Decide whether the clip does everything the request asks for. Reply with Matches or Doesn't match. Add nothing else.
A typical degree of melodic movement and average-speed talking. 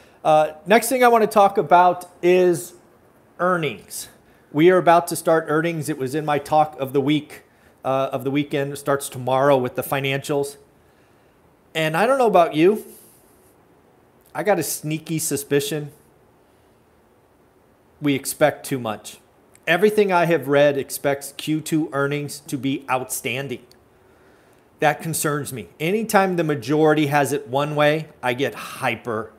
Matches